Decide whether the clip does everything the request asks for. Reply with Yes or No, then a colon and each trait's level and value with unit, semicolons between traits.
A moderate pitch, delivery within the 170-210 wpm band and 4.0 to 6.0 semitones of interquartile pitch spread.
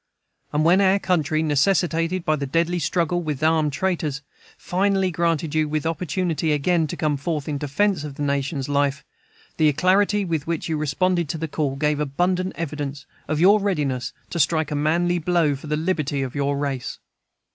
No: medium, 155 Hz; average, 180 wpm; average, 3.4 semitones